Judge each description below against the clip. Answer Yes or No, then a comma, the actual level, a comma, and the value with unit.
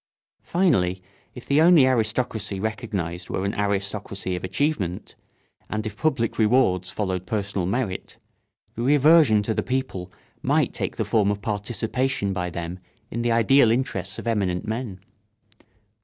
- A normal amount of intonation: Yes, average, 4.8 semitones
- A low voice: Yes, low, 105 Hz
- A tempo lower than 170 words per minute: Yes, average, 140 wpm